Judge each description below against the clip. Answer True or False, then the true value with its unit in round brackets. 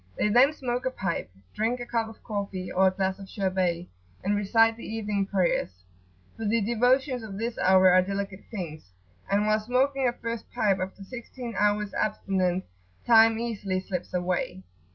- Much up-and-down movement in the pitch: False (3.5 semitones)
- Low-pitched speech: False (205 Hz)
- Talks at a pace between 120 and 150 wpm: False (175 wpm)